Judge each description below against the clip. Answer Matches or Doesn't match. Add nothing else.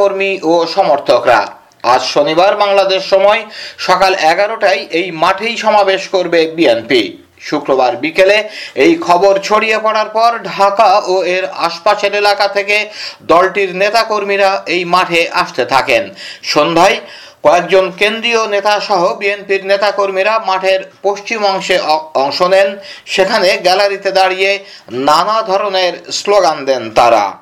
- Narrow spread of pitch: Matches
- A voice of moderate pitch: Doesn't match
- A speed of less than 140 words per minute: Matches